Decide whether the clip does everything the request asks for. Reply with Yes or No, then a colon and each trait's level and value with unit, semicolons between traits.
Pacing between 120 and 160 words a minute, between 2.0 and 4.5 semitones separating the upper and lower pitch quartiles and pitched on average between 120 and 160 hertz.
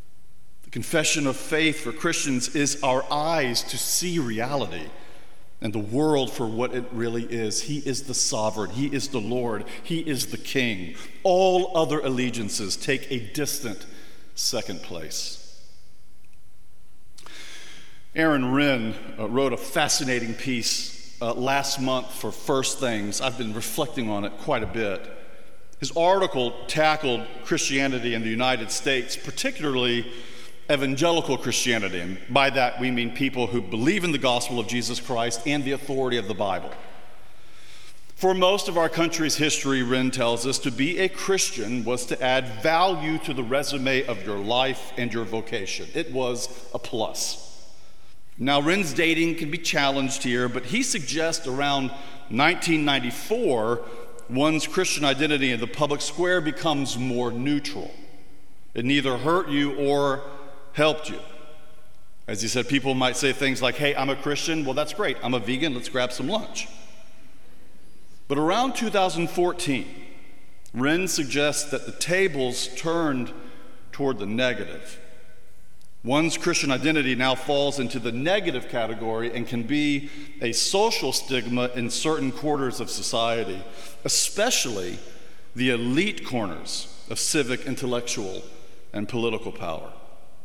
Yes: average, 140 wpm; average, 3.9 semitones; low, 135 Hz